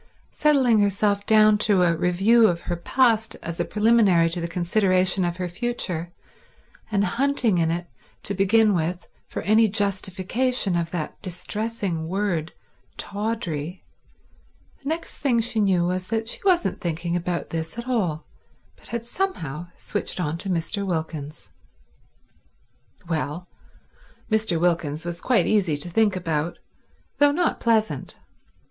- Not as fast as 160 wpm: Yes, average, 140 wpm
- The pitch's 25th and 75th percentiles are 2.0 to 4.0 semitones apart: No, average, 4.5 semitones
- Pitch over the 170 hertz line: Yes, high, 190 Hz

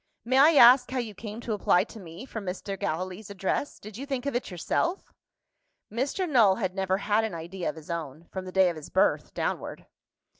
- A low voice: No, high, 205 Hz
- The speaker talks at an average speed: No, fast, 215 wpm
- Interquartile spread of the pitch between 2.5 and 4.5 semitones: No, average, 4.9 semitones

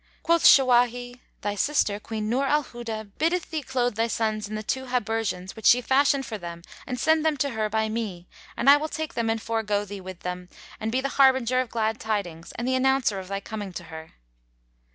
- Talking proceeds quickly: Yes, fast, 215 wpm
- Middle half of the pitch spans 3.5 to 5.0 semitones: Yes, average, 4.1 semitones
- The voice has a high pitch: Yes, high, 225 Hz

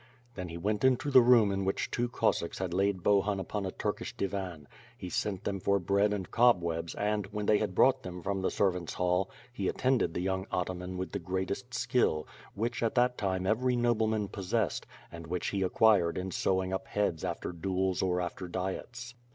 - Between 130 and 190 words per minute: No, average, 200 wpm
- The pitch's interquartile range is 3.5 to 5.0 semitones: No, average, 2.9 semitones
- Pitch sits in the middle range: No, very low, 95 Hz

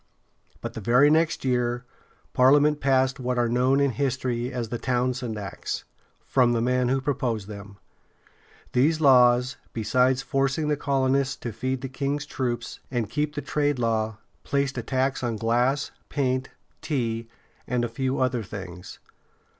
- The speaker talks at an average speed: Yes, average, 155 wpm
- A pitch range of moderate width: No, narrow, 2.3 semitones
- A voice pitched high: No, low, 125 Hz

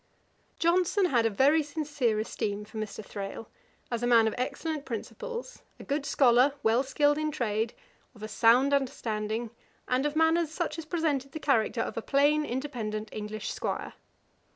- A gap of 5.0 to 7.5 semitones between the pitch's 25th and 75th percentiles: Yes, average, 5.3 semitones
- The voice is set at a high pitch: Yes, very high, 260 Hz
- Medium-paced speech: Yes, average, 170 wpm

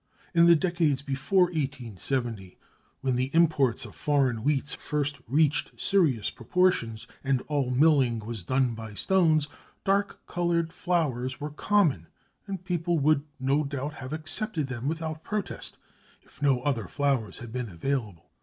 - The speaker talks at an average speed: Yes, average, 145 wpm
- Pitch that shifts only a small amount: No, average, 4.7 semitones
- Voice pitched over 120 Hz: Yes, medium, 140 Hz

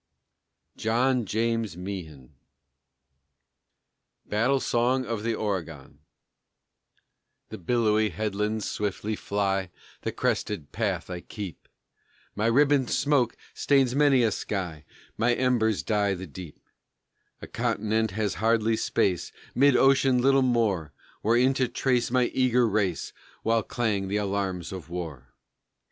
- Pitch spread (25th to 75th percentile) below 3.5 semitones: No, average, 4.2 semitones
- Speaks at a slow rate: Yes, slow, 120 wpm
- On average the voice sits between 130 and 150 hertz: No, low, 110 Hz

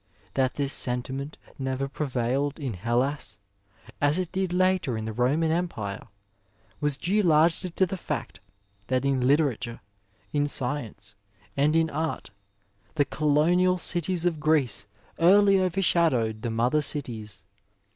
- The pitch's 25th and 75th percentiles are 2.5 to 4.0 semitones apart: No, average, 5.1 semitones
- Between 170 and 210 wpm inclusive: No, slow, 135 wpm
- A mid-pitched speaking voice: Yes, medium, 145 Hz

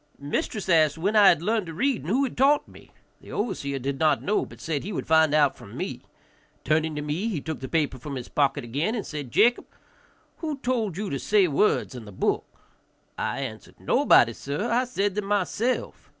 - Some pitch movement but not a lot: No, wide, 6.9 semitones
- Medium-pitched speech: Yes, medium, 165 Hz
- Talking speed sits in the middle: No, fast, 210 wpm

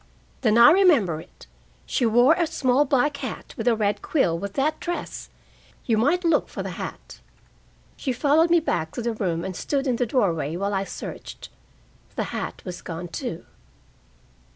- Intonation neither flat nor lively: No, wide, 6.9 semitones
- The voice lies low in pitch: No, high, 240 Hz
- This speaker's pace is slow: No, average, 175 wpm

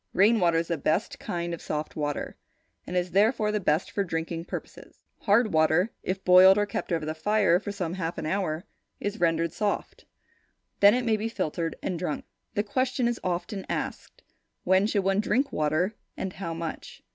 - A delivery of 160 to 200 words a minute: Yes, average, 190 wpm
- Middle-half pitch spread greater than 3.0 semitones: Yes, average, 4.0 semitones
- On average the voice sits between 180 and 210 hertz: Yes, medium, 185 Hz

